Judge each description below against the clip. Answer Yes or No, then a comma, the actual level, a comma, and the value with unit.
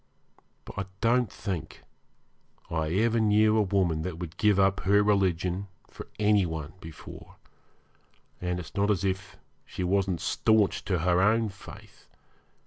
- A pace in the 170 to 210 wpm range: No, average, 145 wpm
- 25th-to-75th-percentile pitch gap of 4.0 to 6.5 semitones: No, average, 2.8 semitones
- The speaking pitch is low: Yes, very low, 95 Hz